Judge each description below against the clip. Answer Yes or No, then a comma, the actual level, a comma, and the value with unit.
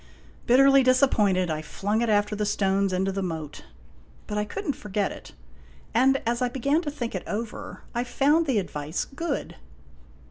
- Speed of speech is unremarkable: Yes, average, 175 wpm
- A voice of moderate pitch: No, high, 220 Hz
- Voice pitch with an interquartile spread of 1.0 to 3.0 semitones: No, wide, 5.5 semitones